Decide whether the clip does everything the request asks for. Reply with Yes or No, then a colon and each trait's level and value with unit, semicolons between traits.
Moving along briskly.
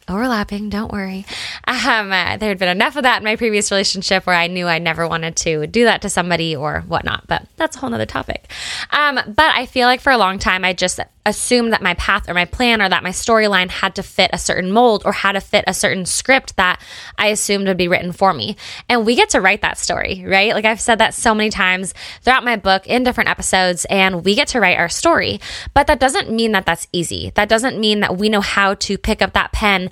Yes: fast, 250 wpm